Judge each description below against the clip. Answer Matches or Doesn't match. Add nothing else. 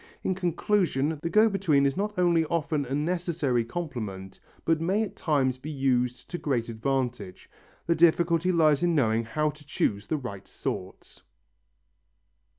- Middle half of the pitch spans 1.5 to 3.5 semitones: Doesn't match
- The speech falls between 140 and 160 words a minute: Matches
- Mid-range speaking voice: Matches